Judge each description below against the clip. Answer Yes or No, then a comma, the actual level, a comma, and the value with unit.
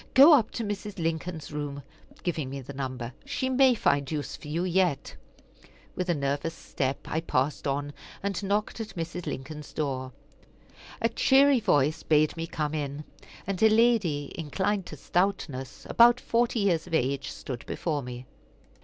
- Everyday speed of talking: Yes, average, 160 wpm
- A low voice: No, medium, 160 Hz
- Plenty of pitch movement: Yes, wide, 6.0 semitones